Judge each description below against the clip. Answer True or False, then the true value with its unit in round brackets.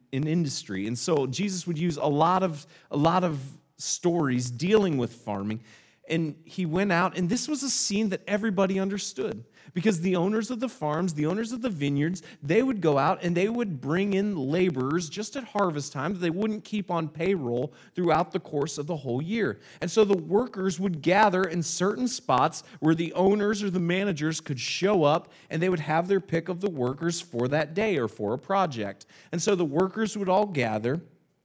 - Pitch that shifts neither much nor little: True (4.8 semitones)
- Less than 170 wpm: False (205 wpm)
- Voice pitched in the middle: True (175 Hz)